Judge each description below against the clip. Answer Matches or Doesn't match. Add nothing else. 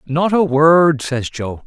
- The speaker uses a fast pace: Doesn't match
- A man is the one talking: Matches